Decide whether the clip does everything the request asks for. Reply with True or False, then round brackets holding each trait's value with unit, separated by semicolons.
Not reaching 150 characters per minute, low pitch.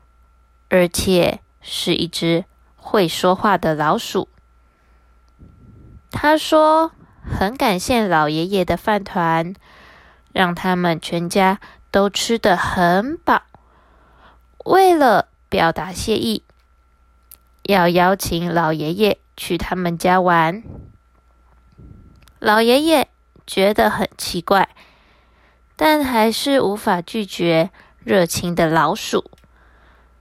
False (135 characters per minute; 175 Hz)